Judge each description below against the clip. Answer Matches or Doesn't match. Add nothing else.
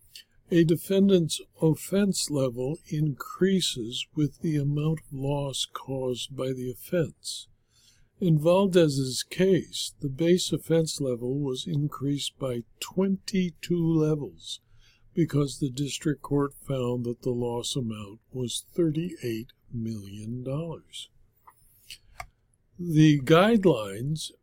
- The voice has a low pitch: Doesn't match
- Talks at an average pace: Doesn't match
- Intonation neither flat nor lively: Matches